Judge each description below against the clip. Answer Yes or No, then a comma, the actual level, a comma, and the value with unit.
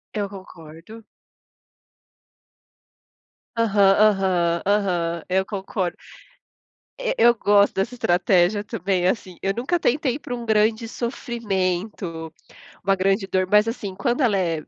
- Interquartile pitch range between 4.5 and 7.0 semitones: No, average, 3.6 semitones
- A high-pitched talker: Yes, high, 195 Hz